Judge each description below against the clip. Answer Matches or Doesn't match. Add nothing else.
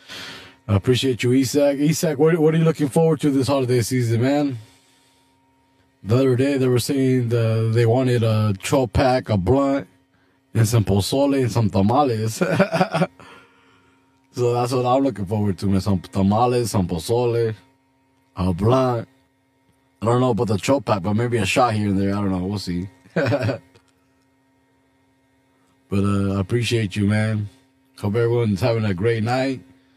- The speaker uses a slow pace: Doesn't match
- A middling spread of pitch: Matches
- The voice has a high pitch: Doesn't match